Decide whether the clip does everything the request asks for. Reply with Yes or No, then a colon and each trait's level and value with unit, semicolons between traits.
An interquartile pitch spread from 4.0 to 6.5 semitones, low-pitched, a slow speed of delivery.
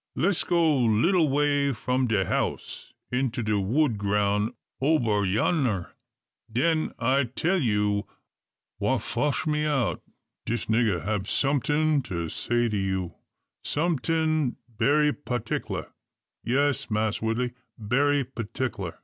Yes: wide, 5.5 semitones; low, 125 Hz; slow, 115 wpm